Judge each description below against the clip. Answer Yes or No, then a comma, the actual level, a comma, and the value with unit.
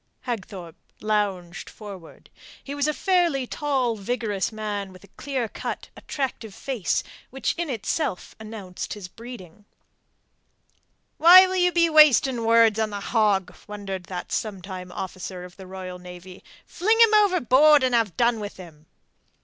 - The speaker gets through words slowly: No, average, 145 wpm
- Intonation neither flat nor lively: No, wide, 6.2 semitones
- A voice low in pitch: No, high, 220 Hz